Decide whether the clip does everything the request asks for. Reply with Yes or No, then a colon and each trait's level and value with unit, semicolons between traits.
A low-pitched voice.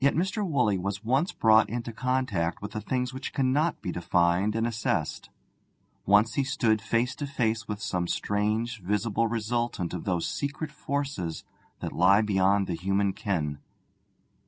Yes: low, 110 Hz